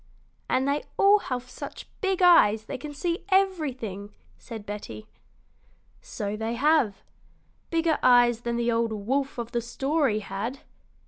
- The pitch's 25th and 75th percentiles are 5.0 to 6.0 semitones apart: Yes, wide, 5.6 semitones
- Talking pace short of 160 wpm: Yes, average, 140 wpm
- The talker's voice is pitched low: No, high, 245 Hz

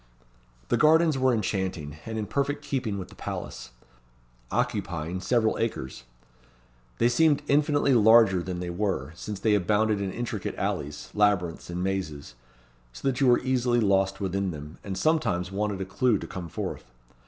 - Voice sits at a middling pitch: No, low, 105 Hz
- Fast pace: No, average, 160 wpm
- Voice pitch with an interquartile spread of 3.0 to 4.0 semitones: No, average, 5.2 semitones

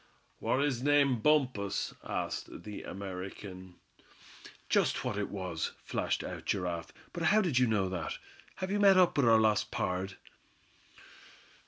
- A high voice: No, low, 105 Hz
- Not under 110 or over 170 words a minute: Yes, average, 145 wpm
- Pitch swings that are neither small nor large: No, wide, 7.4 semitones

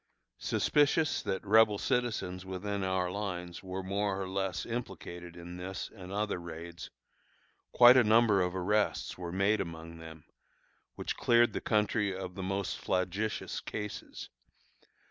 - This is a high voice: No, very low, 95 Hz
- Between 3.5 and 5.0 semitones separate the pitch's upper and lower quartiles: No, average, 2.7 semitones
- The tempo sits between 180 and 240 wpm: No, average, 140 wpm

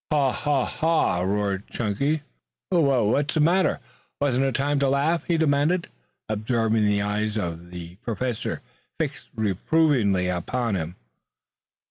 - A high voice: No, low, 120 Hz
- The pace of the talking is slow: Yes, slow, 130 wpm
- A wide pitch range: Yes, wide, 6.1 semitones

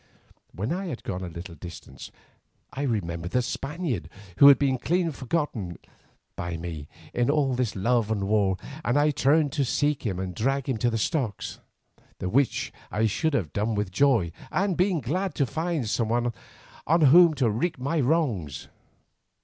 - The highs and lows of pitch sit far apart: Yes, wide, 6.8 semitones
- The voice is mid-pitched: No, low, 125 Hz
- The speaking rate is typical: Yes, average, 175 wpm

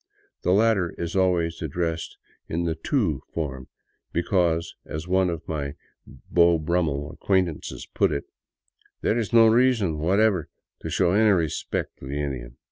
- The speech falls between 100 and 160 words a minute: No, average, 175 wpm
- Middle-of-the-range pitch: No, very low, 85 Hz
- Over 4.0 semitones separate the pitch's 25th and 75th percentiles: No, average, 3.6 semitones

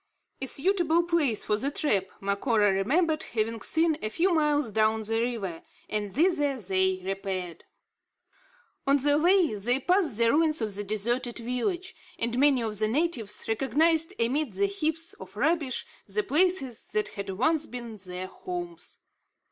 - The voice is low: No, high, 245 Hz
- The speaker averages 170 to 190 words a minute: No, average, 155 wpm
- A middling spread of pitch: No, wide, 7.0 semitones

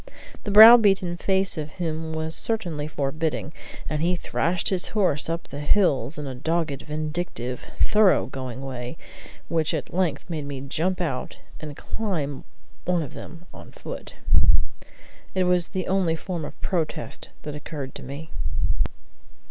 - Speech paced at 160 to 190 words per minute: No, average, 150 wpm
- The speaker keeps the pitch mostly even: No, average, 3.7 semitones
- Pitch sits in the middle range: Yes, medium, 160 Hz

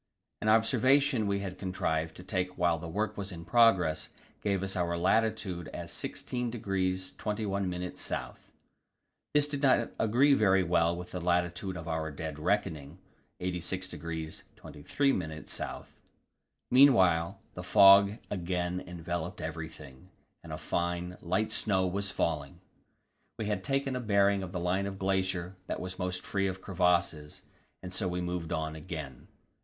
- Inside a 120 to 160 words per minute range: Yes, average, 150 wpm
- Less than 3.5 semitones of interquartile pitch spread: Yes, average, 2.8 semitones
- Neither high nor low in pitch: No, very low, 90 Hz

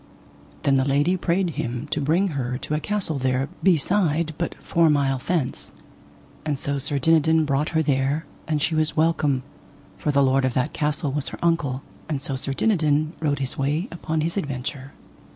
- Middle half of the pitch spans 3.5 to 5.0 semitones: No, average, 2.9 semitones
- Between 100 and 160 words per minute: No, average, 185 wpm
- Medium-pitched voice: Yes, medium, 150 Hz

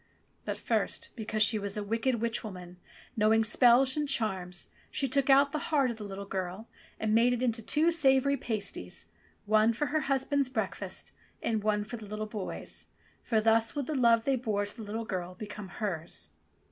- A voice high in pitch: Yes, high, 225 Hz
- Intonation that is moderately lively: Yes, average, 4.0 semitones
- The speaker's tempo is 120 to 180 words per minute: No, average, 200 wpm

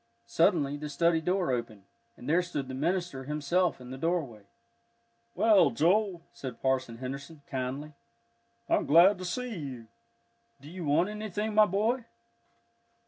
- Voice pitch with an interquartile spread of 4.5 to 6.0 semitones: Yes, wide, 5.6 semitones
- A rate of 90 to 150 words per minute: Yes, average, 140 wpm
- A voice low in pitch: No, medium, 155 Hz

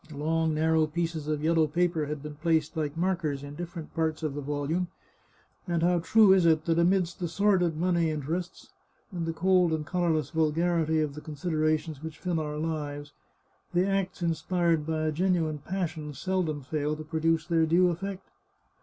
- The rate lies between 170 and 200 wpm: Yes, average, 180 wpm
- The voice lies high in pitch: No, medium, 160 Hz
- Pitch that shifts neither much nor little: No, narrow, 2.3 semitones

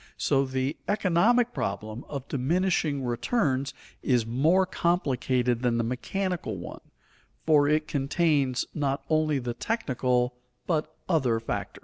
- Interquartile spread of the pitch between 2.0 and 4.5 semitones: No, average, 5.0 semitones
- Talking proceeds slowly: Yes, slow, 120 wpm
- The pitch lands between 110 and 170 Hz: Yes, medium, 140 Hz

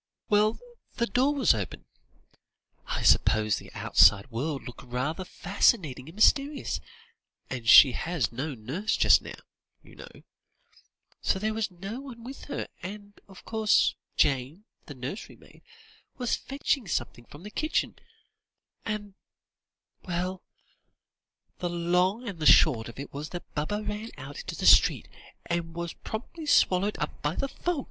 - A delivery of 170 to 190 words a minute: No, average, 150 wpm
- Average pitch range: No, wide, 7.4 semitones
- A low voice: No, medium, 180 Hz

